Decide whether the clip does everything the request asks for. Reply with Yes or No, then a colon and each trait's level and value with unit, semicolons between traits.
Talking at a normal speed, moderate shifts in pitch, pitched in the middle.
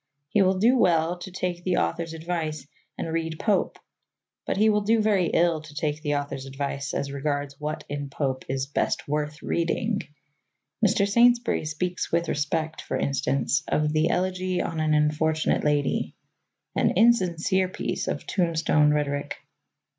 Yes: average, 155 wpm; average, 3.8 semitones; medium, 160 Hz